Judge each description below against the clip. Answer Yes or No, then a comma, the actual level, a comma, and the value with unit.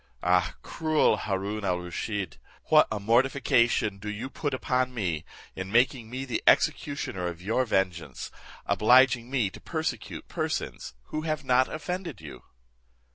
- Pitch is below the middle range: Yes, low, 115 Hz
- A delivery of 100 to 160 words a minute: Yes, average, 140 wpm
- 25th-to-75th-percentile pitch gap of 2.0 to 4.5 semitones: No, wide, 5.5 semitones